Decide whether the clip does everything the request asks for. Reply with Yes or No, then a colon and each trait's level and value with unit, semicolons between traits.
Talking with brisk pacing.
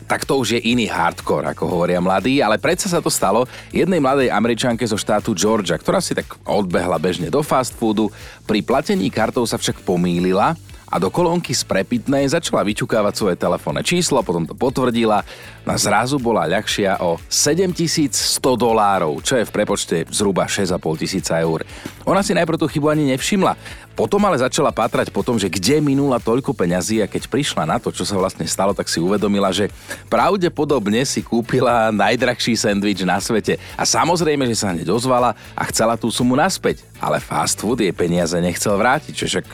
Yes: fast, 180 wpm